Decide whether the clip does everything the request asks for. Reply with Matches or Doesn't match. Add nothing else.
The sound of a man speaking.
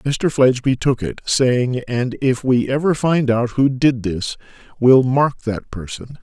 Matches